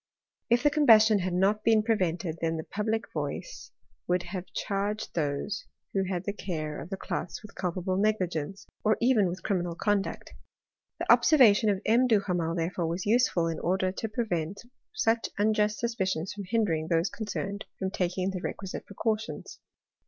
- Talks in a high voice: Yes, high, 195 Hz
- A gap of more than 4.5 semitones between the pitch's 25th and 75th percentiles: No, average, 3.5 semitones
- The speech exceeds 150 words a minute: Yes, average, 165 wpm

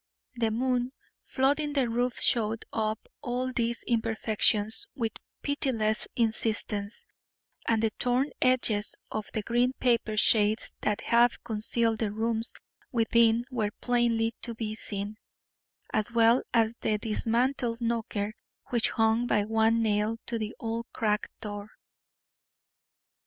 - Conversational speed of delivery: No, slow, 125 wpm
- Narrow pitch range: Yes, narrow, 1.8 semitones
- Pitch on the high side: Yes, high, 225 Hz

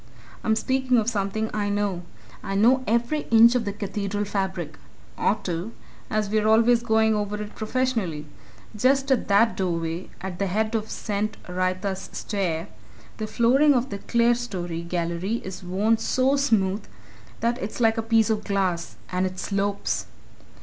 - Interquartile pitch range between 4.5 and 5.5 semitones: No, average, 3.3 semitones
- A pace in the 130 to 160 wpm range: Yes, average, 155 wpm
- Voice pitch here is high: Yes, high, 210 Hz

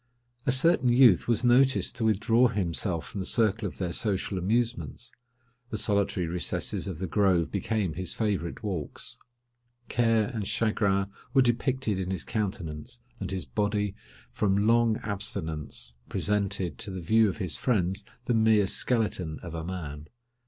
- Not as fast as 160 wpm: Yes, average, 150 wpm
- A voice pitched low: Yes, low, 100 Hz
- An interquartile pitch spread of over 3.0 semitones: Yes, average, 3.6 semitones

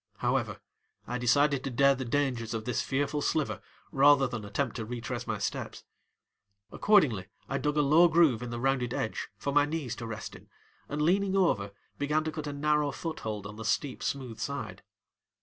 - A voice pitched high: No, medium, 140 Hz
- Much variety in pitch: No, average, 4.1 semitones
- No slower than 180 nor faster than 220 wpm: Yes, average, 190 wpm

